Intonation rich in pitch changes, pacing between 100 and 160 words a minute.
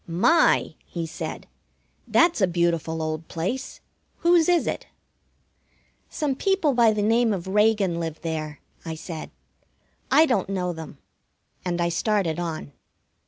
Yes: wide, 6.3 semitones; slow, 135 wpm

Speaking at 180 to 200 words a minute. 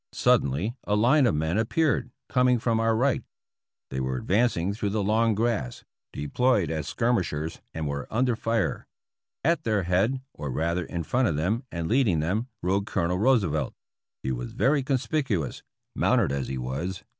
No: average, 170 wpm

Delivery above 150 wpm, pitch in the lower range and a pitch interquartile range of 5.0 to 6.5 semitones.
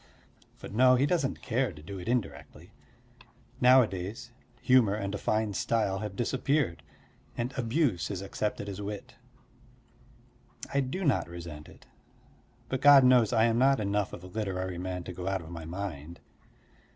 Yes: average, 160 wpm; low, 105 Hz; wide, 5.5 semitones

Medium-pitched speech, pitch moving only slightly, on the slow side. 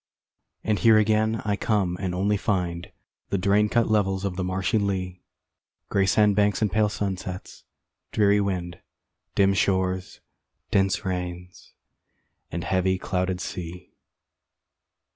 No: very low, 95 Hz; narrow, 2.1 semitones; slow, 125 wpm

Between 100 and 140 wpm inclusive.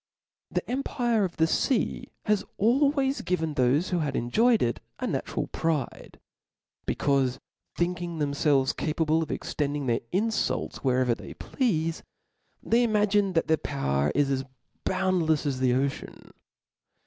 Yes: slow, 135 wpm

